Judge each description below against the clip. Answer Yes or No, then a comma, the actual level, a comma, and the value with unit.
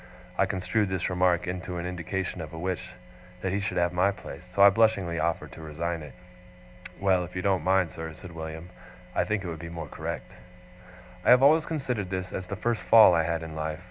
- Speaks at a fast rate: Yes, fast, 220 wpm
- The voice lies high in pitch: No, very low, 90 Hz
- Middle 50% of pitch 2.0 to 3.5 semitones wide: Yes, average, 2.7 semitones